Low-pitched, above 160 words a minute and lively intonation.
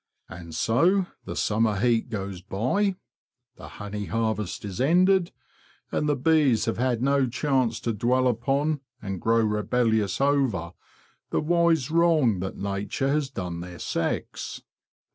No: low, 120 Hz; average, 140 wpm; wide, 5.7 semitones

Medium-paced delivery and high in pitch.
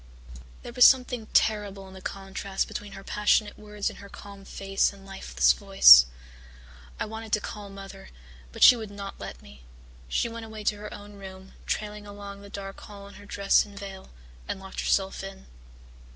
Yes: average, 185 wpm; high, 200 Hz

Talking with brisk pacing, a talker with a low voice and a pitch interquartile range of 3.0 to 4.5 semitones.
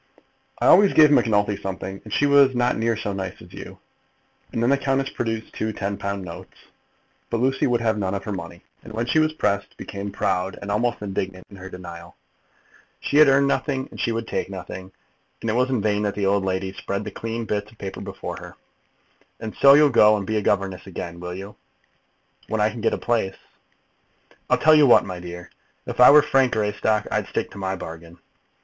Yes: fast, 215 wpm; low, 105 Hz; average, 4.1 semitones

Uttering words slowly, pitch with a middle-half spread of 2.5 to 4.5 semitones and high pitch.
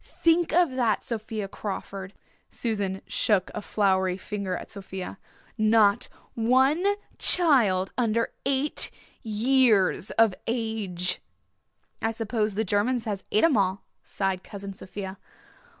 Yes: slow, 120 wpm; average, 3.5 semitones; high, 215 Hz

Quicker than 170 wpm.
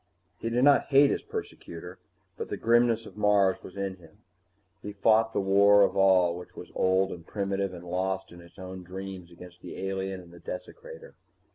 Yes: average, 190 wpm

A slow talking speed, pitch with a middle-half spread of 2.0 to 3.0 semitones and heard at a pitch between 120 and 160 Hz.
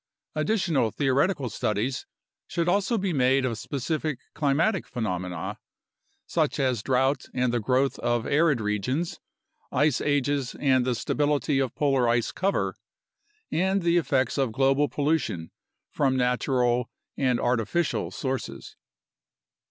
No: slow, 120 wpm; average, 3.5 semitones; low, 135 Hz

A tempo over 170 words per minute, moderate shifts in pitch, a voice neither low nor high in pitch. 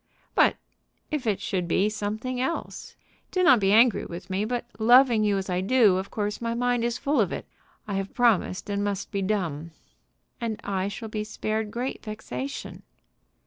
No: average, 185 wpm; average, 3.4 semitones; high, 215 Hz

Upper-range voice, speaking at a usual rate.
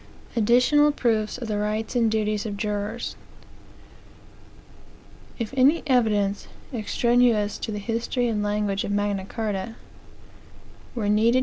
No: high, 220 Hz; slow, 120 wpm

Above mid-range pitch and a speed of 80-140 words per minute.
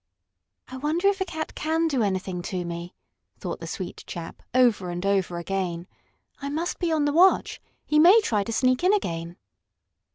No: very high, 255 Hz; average, 185 wpm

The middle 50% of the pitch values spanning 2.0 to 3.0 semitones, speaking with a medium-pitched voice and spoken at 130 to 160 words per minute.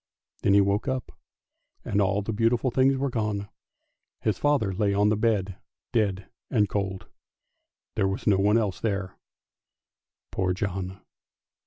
No: narrow, 2.6 semitones; low, 100 Hz; average, 150 wpm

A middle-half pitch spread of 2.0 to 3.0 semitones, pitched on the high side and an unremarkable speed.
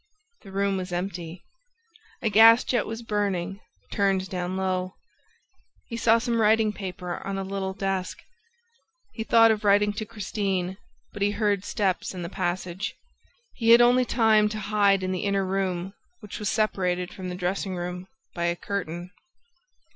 Yes: narrow, 2.6 semitones; high, 195 Hz; average, 160 wpm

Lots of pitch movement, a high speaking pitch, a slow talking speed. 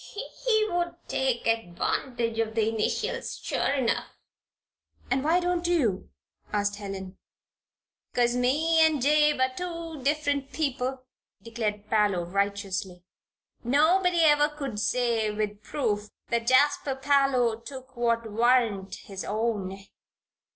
Yes: wide, 5.7 semitones; high, 245 Hz; slow, 115 wpm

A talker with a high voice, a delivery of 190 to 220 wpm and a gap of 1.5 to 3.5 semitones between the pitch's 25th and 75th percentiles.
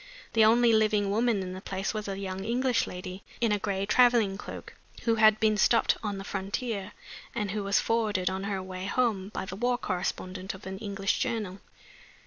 Yes: high, 200 Hz; average, 195 wpm; average, 2.8 semitones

